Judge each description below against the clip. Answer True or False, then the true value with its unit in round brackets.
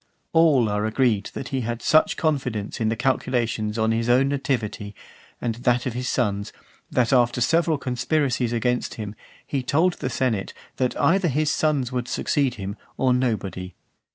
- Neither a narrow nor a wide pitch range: True (3.4 semitones)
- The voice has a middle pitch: False (125 Hz)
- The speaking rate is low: False (170 wpm)